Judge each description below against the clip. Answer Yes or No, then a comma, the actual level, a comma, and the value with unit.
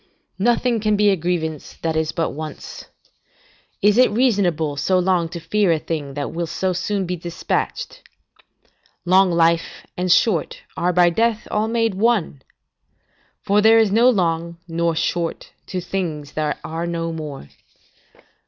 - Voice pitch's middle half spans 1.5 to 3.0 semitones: No, average, 3.9 semitones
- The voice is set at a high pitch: No, medium, 175 Hz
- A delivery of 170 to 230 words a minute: No, average, 155 wpm